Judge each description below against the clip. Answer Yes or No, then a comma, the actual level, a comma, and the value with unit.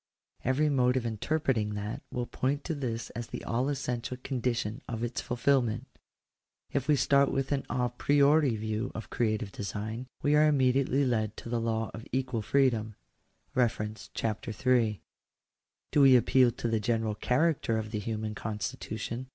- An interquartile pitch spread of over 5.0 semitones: No, average, 3.3 semitones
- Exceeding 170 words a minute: No, average, 160 wpm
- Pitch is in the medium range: No, low, 120 Hz